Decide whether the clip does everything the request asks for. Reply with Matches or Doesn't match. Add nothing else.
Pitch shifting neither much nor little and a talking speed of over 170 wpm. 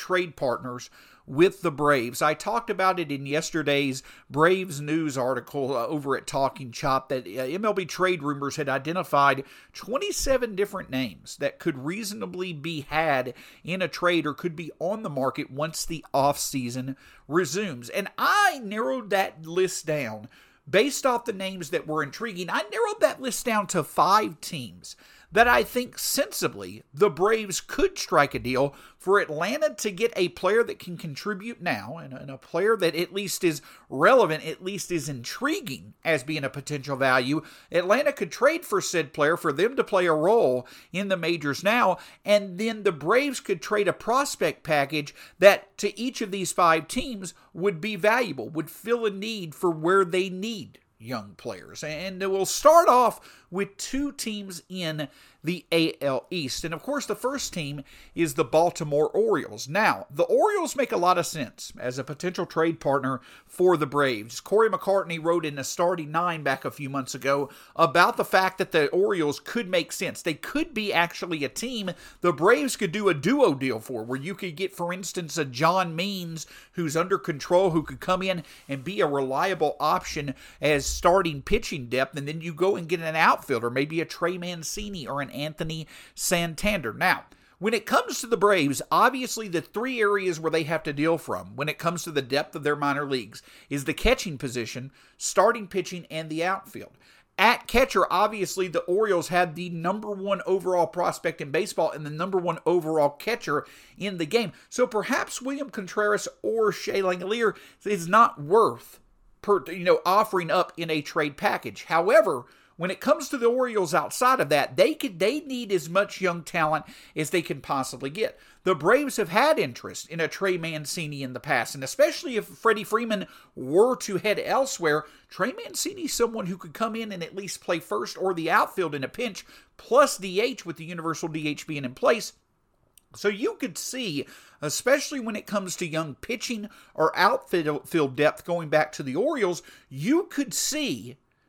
Doesn't match